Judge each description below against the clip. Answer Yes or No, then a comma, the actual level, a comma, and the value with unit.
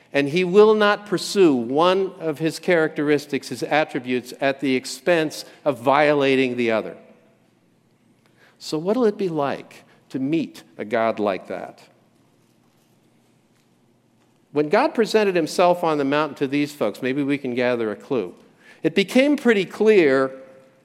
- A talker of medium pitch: Yes, medium, 150 Hz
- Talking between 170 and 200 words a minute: No, average, 140 wpm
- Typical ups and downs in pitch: No, wide, 6.0 semitones